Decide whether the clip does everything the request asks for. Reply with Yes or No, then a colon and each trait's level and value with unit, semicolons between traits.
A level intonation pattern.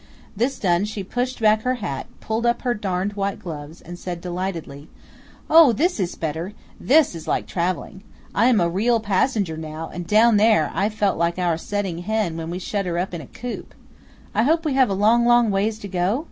No: average, 4.7 semitones